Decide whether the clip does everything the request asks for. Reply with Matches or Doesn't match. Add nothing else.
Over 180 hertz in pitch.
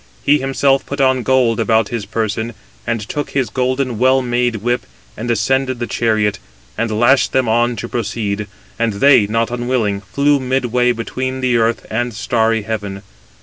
Doesn't match